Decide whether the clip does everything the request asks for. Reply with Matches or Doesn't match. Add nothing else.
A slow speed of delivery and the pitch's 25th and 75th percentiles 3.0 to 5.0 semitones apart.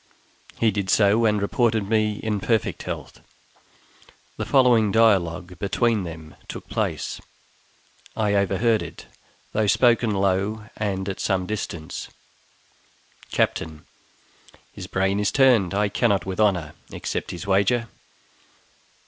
Doesn't match